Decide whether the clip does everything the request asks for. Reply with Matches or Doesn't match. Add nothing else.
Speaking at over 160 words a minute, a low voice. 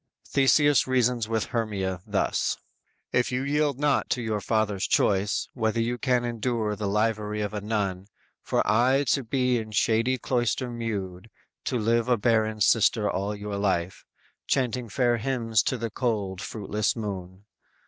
Doesn't match